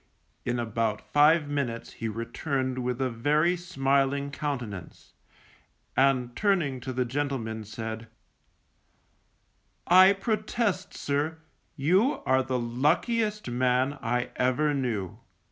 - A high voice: No, low, 135 Hz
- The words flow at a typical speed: No, slow, 110 wpm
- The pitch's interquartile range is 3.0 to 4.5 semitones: Yes, average, 4.0 semitones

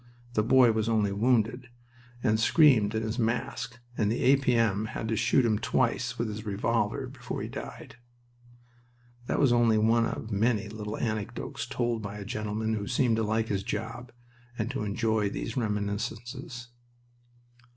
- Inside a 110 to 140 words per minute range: No, average, 160 wpm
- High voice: No, low, 110 Hz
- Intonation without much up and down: Yes, narrow, 2.1 semitones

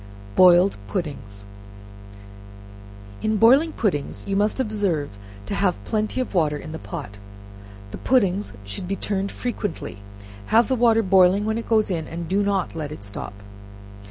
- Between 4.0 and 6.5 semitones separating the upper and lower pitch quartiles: Yes, wide, 5.5 semitones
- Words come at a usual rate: Yes, average, 155 wpm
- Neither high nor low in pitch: No, high, 195 Hz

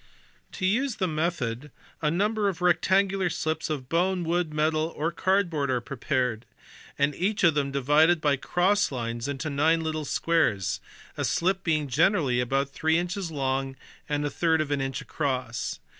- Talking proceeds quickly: No, average, 165 wpm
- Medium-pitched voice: Yes, medium, 155 Hz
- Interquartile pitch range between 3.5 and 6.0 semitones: Yes, average, 4.3 semitones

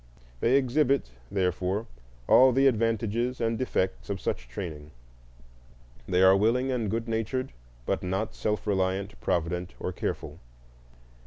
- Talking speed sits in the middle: No, slow, 130 wpm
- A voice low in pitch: Yes, low, 110 Hz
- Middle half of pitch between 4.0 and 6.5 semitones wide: Yes, average, 4.6 semitones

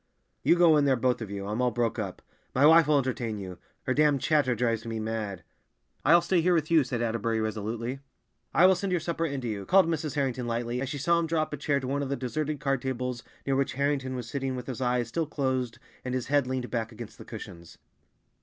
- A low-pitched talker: Yes, low, 130 Hz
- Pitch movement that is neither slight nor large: Yes, average, 4.0 semitones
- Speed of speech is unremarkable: No, fast, 245 wpm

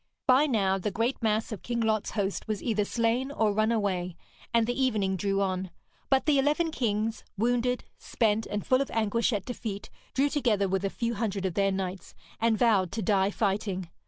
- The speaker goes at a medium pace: Yes, average, 195 wpm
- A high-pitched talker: Yes, high, 215 Hz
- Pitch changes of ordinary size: Yes, average, 3.3 semitones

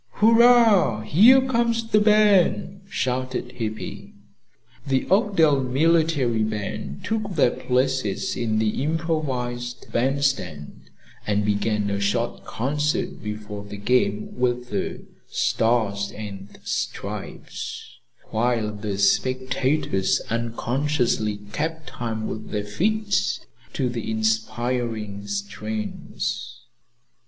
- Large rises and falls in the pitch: Yes, wide, 5.8 semitones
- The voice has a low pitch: Yes, low, 120 Hz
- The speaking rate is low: Yes, slow, 95 wpm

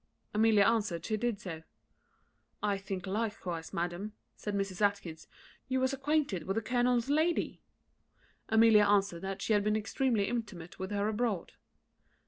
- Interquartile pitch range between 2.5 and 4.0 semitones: Yes, average, 3.1 semitones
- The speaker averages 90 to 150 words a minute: Yes, average, 145 wpm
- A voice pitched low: No, high, 210 Hz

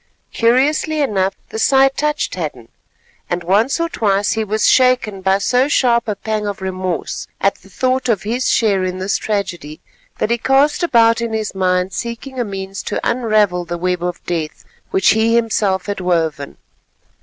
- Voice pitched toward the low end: No, high, 210 Hz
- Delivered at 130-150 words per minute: No, average, 175 wpm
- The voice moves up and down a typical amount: Yes, average, 4.1 semitones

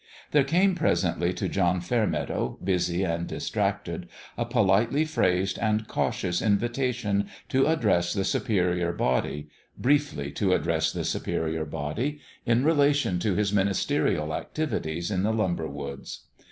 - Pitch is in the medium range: No, low, 100 Hz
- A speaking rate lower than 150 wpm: Yes, slow, 135 wpm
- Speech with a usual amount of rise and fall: No, wide, 6.2 semitones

